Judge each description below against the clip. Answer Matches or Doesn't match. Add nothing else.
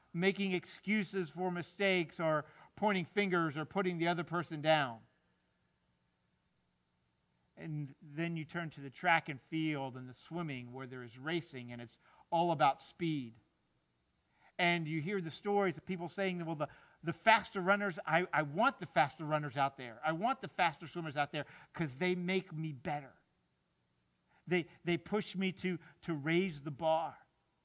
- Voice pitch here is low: Doesn't match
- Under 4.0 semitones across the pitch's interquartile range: Doesn't match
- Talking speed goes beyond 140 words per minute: Matches